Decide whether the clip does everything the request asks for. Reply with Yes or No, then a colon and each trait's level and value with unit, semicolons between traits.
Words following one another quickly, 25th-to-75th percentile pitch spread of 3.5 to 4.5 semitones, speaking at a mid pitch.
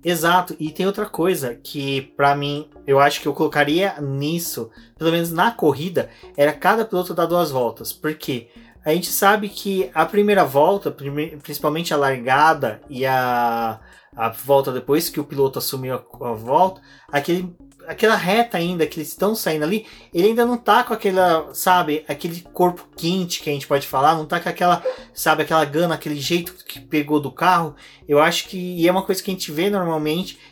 Yes: fast, 190 wpm; average, 4.2 semitones; medium, 160 Hz